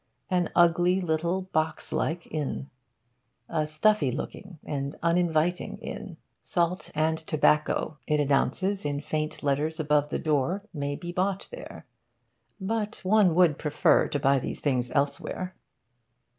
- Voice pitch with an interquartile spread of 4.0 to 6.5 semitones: No, average, 3.6 semitones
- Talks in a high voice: No, medium, 160 Hz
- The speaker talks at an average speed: No, slow, 130 wpm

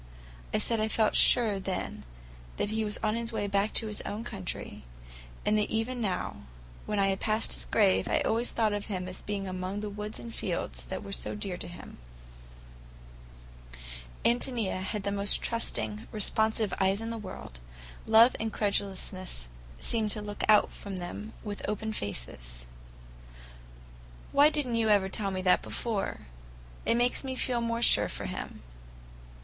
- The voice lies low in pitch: No, high, 210 Hz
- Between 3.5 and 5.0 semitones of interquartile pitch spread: No, average, 2.7 semitones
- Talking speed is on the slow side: No, average, 170 wpm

